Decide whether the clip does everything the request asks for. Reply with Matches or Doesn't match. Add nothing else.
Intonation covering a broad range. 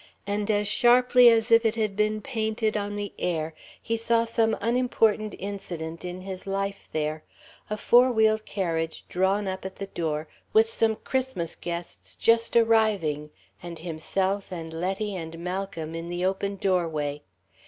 Doesn't match